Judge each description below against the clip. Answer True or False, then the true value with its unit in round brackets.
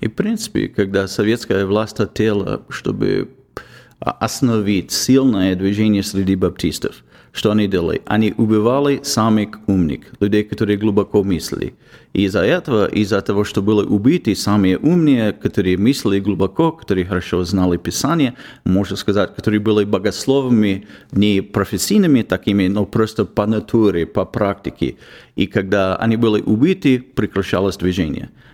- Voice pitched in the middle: False (105 Hz)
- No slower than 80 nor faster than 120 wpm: False (130 wpm)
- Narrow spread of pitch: True (2.3 semitones)